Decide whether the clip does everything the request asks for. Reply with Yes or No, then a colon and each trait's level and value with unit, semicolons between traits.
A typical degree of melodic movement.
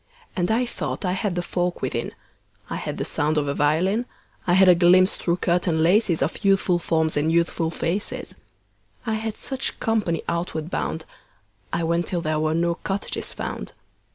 Yes: average, 3.0 semitones